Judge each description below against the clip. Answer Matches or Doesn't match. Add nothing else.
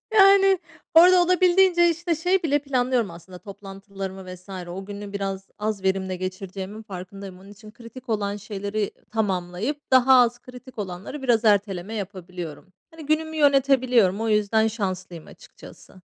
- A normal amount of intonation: Doesn't match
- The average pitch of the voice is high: Matches